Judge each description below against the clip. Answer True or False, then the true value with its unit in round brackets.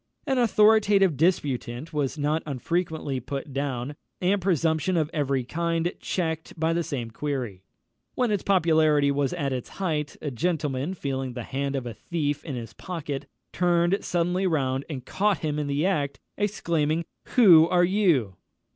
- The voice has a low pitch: False (155 Hz)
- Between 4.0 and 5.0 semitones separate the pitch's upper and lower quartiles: True (4.3 semitones)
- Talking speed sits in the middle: True (155 wpm)